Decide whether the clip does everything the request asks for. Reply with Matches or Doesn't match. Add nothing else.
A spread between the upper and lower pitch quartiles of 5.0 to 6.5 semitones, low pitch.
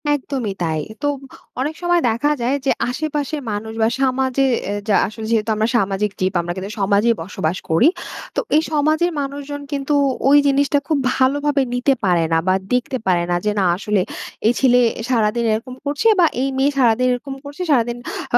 Doesn't match